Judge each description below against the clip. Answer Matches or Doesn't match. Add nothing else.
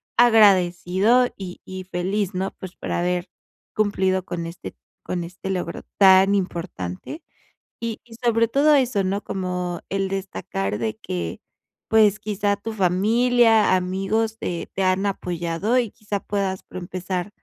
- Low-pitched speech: Doesn't match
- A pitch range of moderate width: Matches